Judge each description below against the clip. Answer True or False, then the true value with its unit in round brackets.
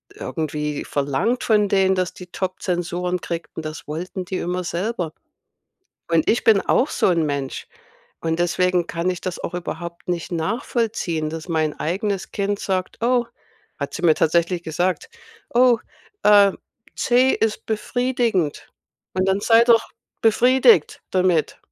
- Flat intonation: False (4.2 semitones)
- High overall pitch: False (180 Hz)